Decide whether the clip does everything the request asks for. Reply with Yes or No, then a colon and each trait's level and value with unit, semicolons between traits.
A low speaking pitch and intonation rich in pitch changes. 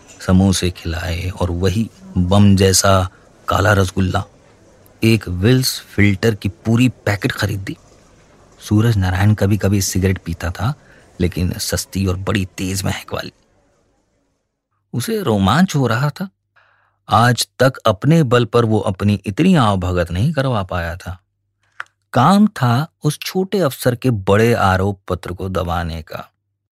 No: low, 100 Hz; average, 4.1 semitones